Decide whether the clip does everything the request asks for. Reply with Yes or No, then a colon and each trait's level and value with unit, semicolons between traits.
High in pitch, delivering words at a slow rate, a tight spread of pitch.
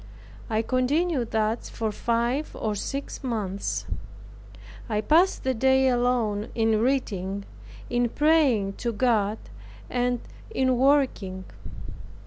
No: high, 240 Hz; slow, 110 wpm; average, 3.6 semitones